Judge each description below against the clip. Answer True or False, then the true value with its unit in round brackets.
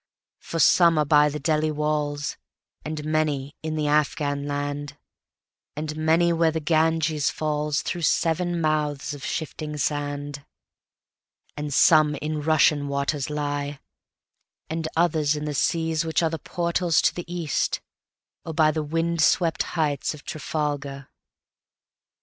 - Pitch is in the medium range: True (150 Hz)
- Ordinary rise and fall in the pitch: False (1.7 semitones)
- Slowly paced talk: True (120 wpm)